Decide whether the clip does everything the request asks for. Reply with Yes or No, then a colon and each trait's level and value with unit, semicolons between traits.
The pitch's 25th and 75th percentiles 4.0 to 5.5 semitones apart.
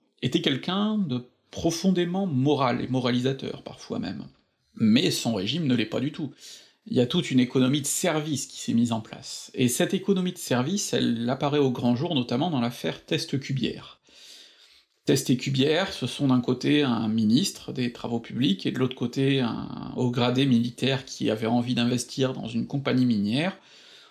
No: average, 3.3 semitones